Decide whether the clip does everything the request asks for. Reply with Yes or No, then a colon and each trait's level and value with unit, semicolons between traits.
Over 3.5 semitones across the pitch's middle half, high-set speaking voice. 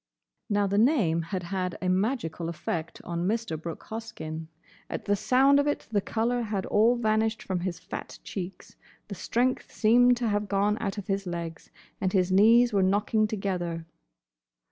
Yes: average, 3.9 semitones; high, 200 Hz